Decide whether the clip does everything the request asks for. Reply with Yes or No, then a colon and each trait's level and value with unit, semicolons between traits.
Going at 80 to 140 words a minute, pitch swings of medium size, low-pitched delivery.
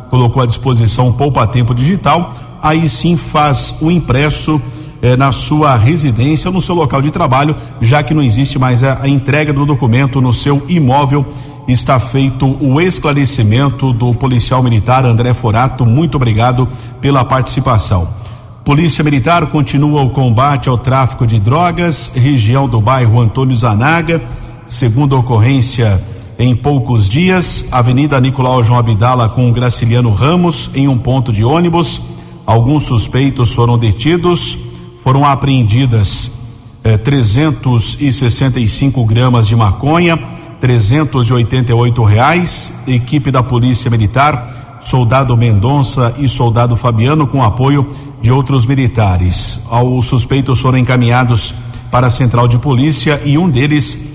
Yes: average, 130 wpm; average, 3.0 semitones; low, 130 Hz